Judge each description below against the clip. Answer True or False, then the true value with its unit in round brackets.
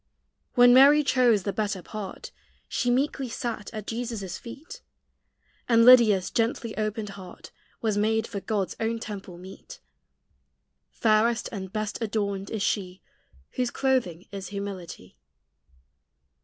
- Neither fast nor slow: False (125 wpm)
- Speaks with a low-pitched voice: False (215 Hz)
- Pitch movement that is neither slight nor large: True (3.2 semitones)